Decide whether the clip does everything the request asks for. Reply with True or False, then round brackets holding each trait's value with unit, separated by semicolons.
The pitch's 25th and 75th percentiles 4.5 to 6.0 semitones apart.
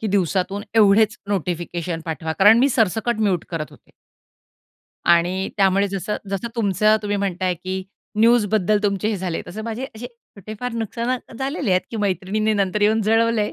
False (3.0 semitones)